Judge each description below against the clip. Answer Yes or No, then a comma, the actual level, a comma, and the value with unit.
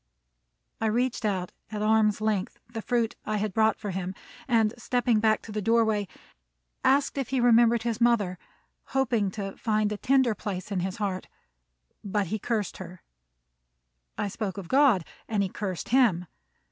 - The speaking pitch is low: No, high, 215 Hz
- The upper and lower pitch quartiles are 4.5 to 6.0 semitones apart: No, average, 2.9 semitones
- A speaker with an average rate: Yes, average, 165 wpm